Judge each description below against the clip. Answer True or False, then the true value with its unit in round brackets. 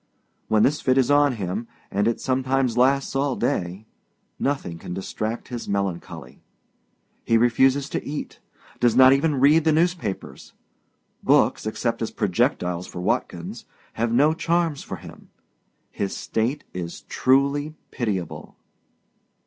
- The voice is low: True (130 Hz)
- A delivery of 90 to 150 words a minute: True (135 wpm)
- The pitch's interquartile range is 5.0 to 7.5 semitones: True (5.4 semitones)